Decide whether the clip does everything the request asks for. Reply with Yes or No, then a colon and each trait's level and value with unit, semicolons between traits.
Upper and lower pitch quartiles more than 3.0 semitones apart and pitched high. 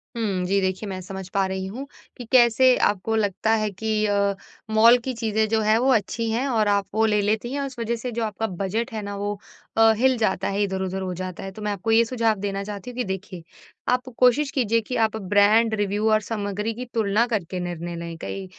No: average, 2.7 semitones; high, 215 Hz